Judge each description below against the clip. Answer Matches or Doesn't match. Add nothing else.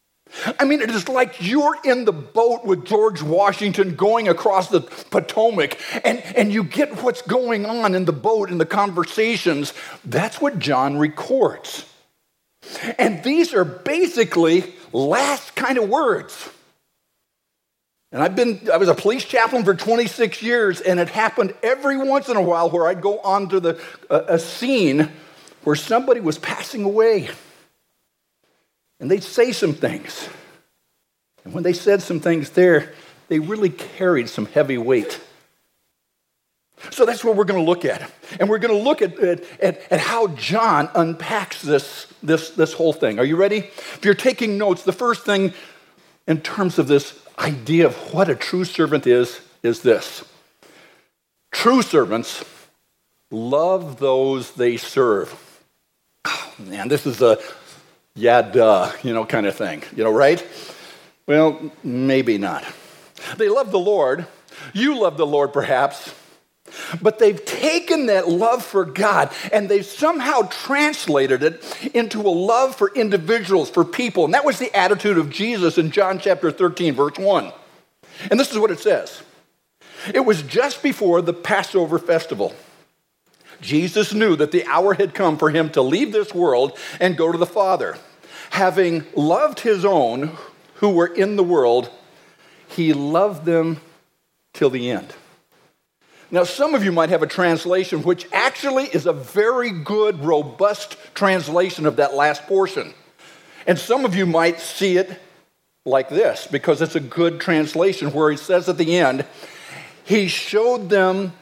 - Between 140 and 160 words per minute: Matches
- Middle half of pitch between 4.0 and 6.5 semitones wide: Matches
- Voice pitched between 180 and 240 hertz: Matches